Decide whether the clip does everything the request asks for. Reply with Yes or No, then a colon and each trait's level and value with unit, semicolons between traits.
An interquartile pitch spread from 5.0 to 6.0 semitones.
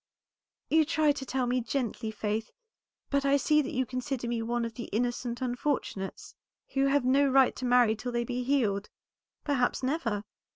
No: average, 2.7 semitones